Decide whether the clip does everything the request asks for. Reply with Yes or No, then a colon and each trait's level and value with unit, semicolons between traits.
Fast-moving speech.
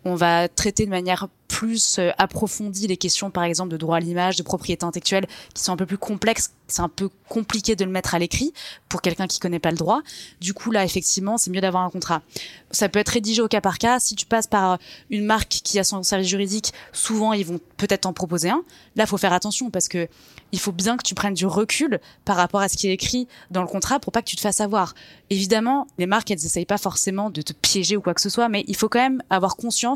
Yes: fast, 260 wpm